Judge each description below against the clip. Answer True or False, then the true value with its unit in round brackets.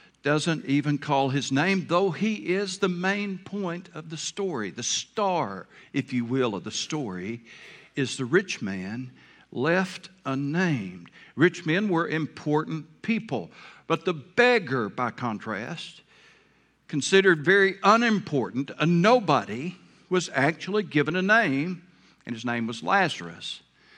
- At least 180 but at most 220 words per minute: False (135 wpm)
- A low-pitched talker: False (165 Hz)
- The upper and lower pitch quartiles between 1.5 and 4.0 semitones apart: False (5.6 semitones)